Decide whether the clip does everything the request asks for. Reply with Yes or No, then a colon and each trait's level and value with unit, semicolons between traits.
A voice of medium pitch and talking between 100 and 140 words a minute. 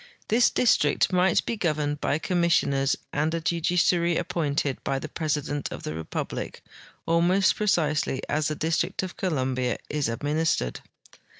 Yes: medium, 155 Hz; slow, 135 wpm